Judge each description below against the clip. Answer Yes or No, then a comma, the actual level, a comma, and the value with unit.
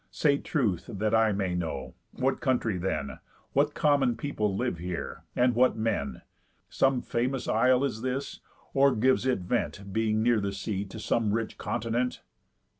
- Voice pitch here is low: Yes, low, 115 Hz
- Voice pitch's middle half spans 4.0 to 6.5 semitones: Yes, average, 4.5 semitones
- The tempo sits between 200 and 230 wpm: No, average, 160 wpm